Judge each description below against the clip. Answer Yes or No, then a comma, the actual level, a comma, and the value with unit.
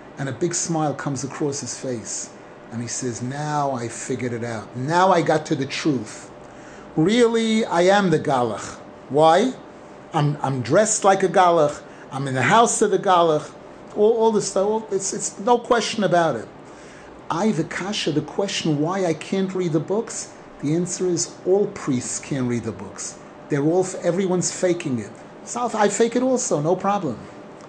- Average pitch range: No, wide, 6.2 semitones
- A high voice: No, medium, 165 Hz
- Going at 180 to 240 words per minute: Yes, average, 185 wpm